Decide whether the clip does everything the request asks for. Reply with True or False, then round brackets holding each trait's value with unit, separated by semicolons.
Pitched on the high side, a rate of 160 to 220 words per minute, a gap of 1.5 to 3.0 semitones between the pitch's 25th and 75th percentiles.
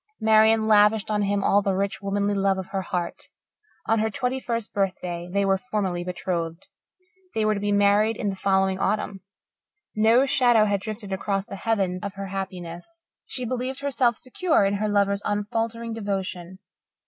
True (205 Hz; 170 wpm; 2.4 semitones)